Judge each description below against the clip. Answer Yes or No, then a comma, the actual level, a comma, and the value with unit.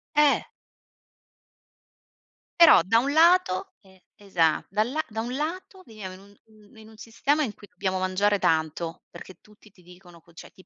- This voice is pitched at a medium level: No, high, 205 Hz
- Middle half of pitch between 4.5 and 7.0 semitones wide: Yes, average, 4.8 semitones